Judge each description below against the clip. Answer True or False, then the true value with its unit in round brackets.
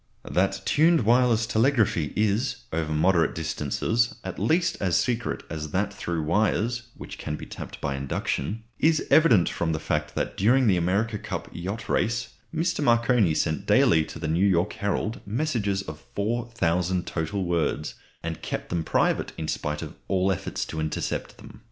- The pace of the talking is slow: False (165 wpm)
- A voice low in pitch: True (100 Hz)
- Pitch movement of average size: False (6.1 semitones)